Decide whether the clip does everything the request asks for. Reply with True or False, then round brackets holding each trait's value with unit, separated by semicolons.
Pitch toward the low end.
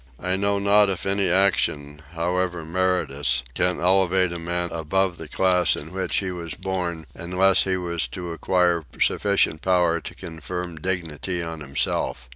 True (90 Hz)